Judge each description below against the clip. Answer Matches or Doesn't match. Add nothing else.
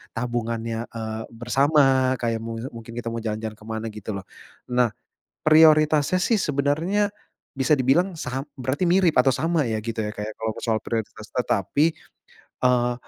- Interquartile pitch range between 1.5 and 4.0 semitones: Doesn't match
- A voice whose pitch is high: Doesn't match